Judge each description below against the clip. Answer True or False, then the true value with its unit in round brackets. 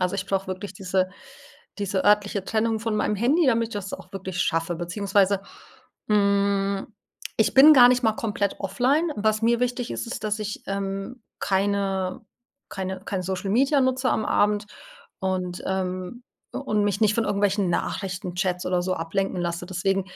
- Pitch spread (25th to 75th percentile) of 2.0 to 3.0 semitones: True (2.6 semitones)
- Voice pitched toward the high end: True (200 Hz)